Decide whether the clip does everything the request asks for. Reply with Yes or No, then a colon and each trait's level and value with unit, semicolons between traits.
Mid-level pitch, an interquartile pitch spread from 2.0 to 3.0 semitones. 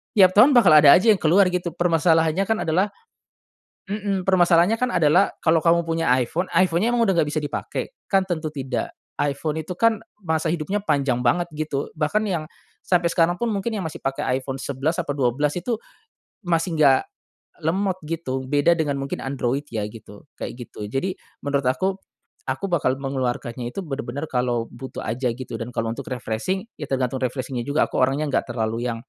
No: medium, 155 Hz; wide, 5.4 semitones